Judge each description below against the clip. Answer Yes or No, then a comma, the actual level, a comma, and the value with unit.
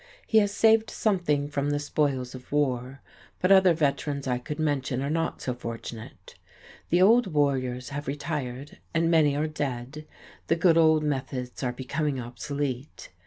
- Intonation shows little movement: No, average, 3.5 semitones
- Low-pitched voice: No, medium, 145 Hz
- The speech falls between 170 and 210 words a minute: No, average, 160 wpm